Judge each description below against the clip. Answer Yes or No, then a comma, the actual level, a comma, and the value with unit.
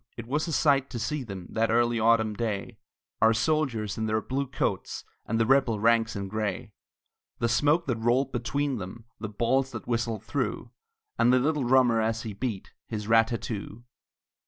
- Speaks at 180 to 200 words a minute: Yes, average, 185 wpm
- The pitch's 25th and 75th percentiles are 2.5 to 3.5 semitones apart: Yes, average, 3.0 semitones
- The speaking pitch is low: Yes, low, 115 Hz